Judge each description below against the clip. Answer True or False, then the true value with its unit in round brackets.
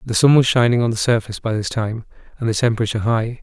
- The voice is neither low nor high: False (115 Hz)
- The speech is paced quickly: True (245 wpm)